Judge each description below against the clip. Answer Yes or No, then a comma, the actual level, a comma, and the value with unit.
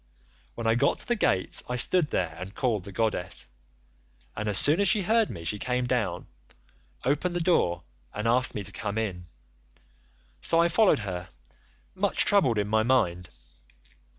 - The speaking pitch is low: Yes, low, 115 Hz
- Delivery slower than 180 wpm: Yes, average, 170 wpm